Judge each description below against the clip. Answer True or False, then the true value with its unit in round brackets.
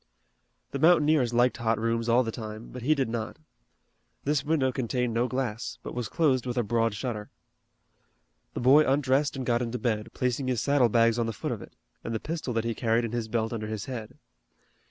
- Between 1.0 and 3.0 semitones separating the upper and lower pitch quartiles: True (2.5 semitones)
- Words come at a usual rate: False (210 wpm)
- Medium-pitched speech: False (120 Hz)